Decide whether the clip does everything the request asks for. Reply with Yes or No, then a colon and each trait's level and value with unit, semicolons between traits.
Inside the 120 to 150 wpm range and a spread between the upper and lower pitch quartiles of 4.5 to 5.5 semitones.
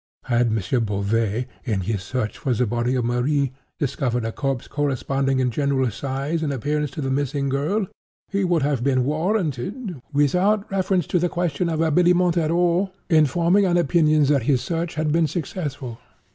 No: average, 175 wpm; average, 4.9 semitones